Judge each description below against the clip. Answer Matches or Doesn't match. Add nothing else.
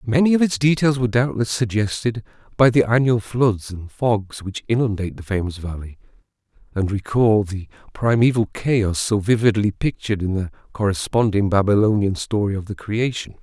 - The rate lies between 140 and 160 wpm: Matches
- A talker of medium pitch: Doesn't match